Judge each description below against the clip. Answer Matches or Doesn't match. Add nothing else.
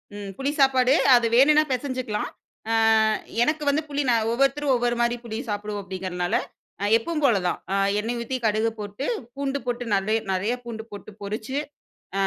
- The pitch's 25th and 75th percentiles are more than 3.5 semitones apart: Matches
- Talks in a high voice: Matches